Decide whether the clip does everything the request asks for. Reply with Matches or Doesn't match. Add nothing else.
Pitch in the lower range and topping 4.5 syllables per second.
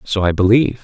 Matches